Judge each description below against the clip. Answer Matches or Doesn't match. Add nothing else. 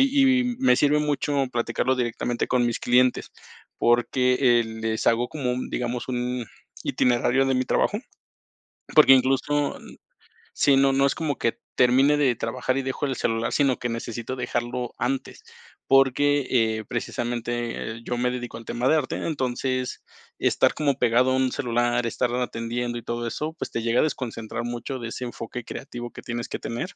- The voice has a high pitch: Doesn't match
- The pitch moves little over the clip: Matches